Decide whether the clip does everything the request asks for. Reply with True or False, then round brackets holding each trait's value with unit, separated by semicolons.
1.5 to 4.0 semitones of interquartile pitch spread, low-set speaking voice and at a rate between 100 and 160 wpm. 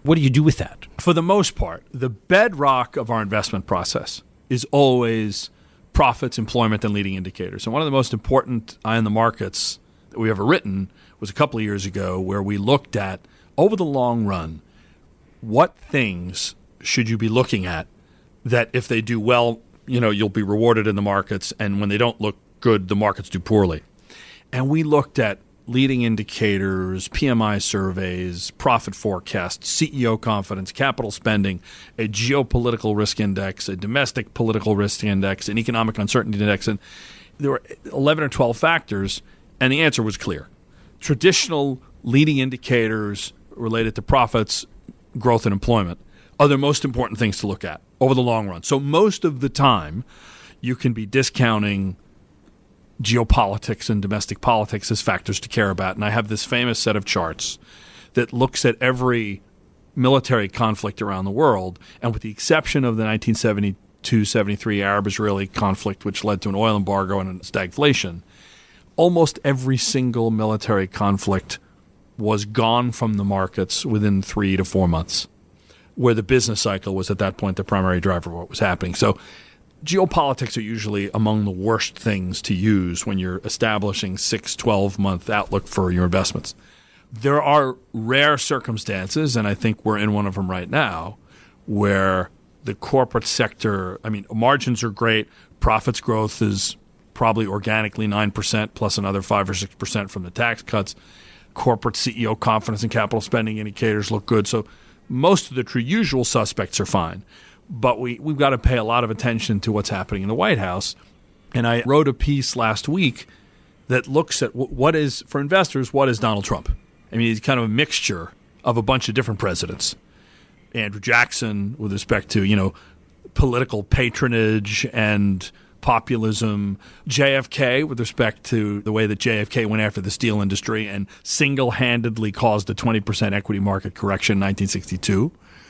False (3.6 semitones; 110 Hz; 170 wpm)